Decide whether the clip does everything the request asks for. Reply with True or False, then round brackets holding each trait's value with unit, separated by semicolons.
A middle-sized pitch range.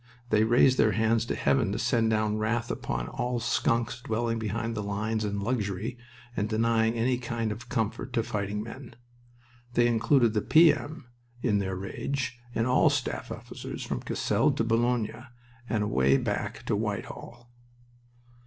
False (2.0 semitones)